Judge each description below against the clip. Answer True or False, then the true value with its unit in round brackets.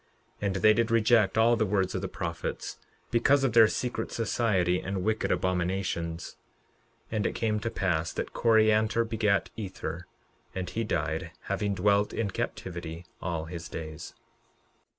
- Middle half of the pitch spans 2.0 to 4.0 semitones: True (3.7 semitones)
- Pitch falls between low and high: False (100 Hz)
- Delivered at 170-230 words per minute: False (155 wpm)